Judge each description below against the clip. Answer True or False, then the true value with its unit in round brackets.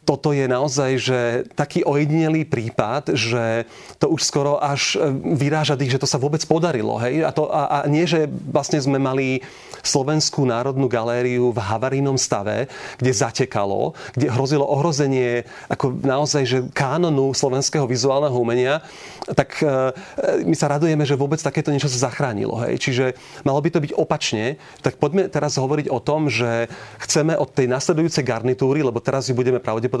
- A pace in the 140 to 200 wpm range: True (160 wpm)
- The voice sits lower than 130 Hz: False (140 Hz)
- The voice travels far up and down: False (2.8 semitones)